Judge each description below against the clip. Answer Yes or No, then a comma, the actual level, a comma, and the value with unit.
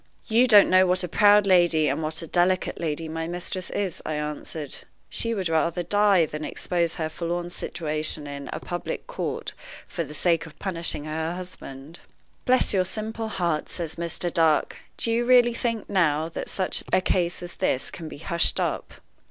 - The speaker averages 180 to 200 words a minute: Yes, average, 185 wpm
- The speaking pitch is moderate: Yes, medium, 175 Hz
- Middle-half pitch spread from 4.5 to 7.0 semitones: No, average, 3.0 semitones